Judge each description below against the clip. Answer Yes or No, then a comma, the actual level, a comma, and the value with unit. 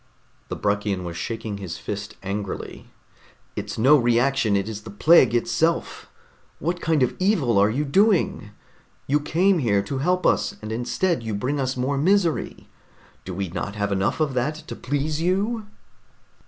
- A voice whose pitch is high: No, low, 130 Hz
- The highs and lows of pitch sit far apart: Yes, wide, 7.6 semitones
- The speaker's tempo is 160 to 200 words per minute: Yes, average, 165 wpm